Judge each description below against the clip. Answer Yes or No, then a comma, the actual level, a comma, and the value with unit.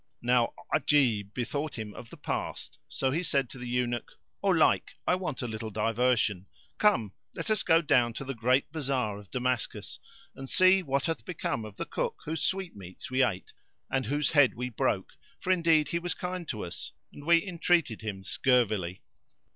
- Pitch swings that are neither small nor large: No, wide, 6.2 semitones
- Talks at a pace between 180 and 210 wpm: Yes, average, 185 wpm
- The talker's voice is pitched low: Yes, low, 130 Hz